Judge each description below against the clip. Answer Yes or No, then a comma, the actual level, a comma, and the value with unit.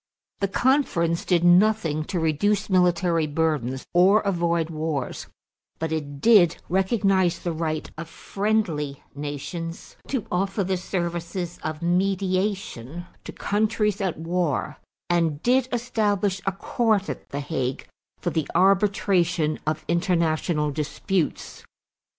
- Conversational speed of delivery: No, slow, 120 wpm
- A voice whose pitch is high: No, medium, 175 Hz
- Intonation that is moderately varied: Yes, average, 3.8 semitones